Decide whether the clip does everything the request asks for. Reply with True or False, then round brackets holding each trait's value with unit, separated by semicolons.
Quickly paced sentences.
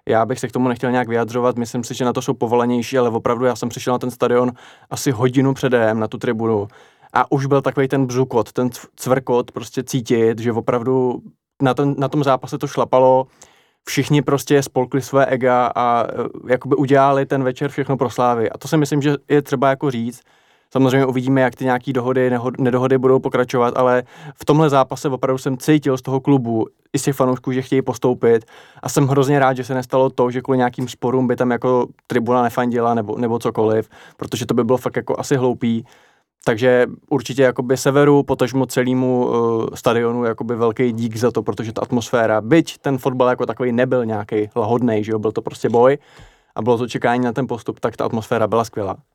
True (205 wpm)